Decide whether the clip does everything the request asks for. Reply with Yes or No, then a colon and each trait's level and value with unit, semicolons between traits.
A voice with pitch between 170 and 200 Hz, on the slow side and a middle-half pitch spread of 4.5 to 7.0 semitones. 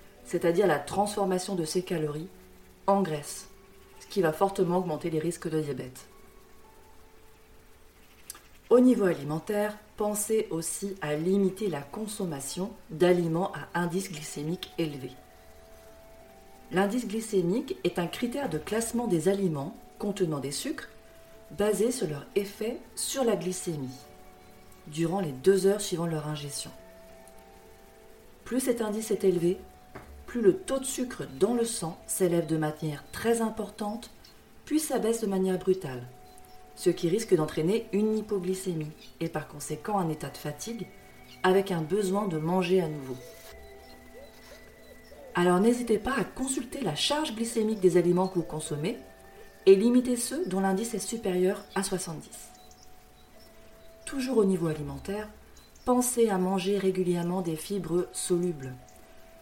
Yes: medium, 185 Hz; slow, 135 wpm; wide, 5.5 semitones